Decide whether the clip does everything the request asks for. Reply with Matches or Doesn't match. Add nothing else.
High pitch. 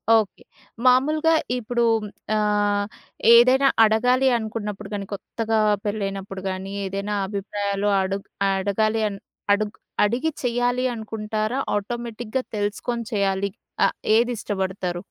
Matches